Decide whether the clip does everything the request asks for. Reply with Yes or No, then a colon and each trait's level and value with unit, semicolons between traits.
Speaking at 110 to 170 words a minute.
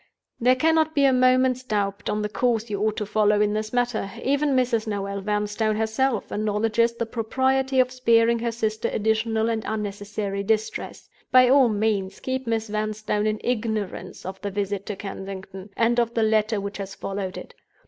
No: average, 180 wpm